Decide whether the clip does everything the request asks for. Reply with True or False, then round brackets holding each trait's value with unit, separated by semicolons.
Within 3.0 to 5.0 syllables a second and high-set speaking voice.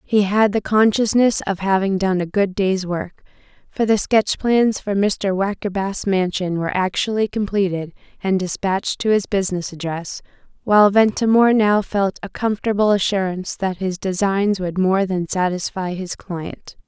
True (4.8 syllables/s; 195 Hz)